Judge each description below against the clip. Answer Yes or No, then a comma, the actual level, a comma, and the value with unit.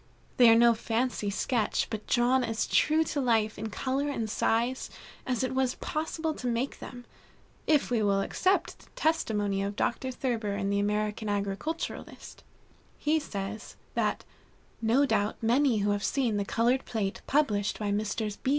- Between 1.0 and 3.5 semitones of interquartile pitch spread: No, average, 4.0 semitones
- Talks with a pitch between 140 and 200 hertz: No, high, 230 Hz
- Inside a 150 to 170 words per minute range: Yes, average, 160 wpm